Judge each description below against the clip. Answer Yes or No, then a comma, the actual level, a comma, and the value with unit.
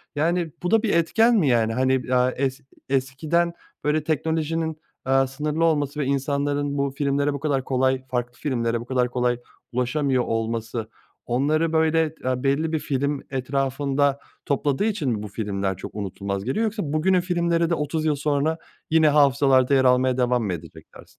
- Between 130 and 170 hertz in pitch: Yes, medium, 140 Hz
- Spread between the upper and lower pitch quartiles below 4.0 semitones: Yes, average, 3.6 semitones